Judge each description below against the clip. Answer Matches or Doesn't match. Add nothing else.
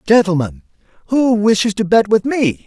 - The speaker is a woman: Doesn't match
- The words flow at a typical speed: Matches